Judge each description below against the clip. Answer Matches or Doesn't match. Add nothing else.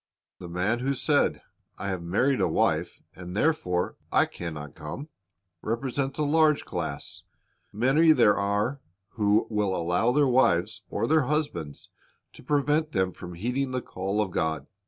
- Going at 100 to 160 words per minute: Matches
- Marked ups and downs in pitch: Matches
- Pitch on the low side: Matches